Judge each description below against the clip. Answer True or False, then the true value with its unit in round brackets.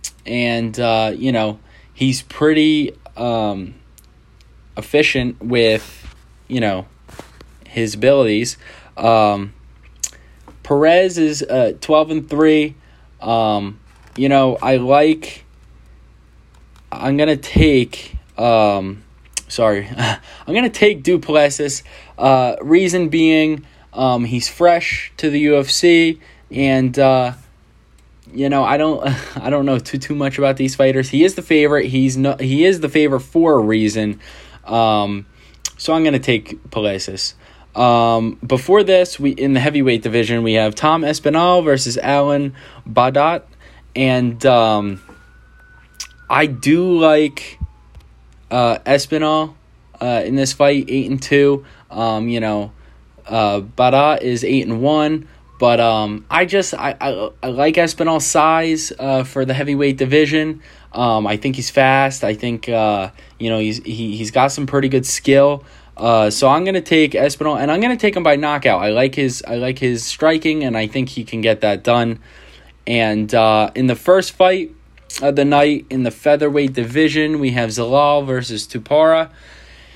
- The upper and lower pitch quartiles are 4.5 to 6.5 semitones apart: True (5.1 semitones)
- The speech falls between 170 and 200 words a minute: False (145 wpm)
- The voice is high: False (130 Hz)